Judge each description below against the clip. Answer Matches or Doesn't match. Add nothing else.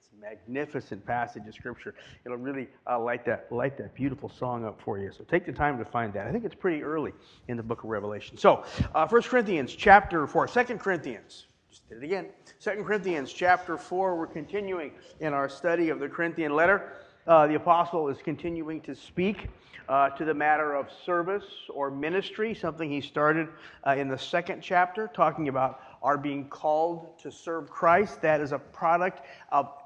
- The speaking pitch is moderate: Matches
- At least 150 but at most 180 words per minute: Doesn't match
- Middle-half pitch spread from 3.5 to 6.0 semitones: Matches